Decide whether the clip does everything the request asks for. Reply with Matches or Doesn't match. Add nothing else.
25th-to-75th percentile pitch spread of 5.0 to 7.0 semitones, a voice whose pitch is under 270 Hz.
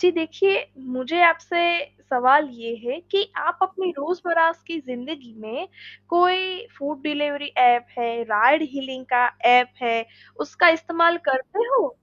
Doesn't match